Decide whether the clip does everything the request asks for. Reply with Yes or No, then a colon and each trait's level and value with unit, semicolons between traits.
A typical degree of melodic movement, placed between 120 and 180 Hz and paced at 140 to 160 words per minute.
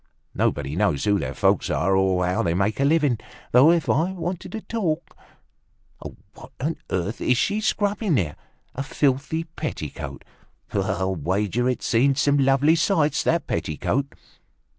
No: wide, 9.0 semitones; low, 135 Hz; average, 150 wpm